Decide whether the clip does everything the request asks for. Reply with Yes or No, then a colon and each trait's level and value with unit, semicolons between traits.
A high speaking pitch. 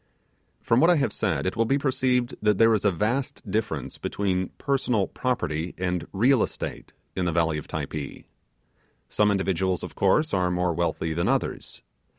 No: very low, 95 Hz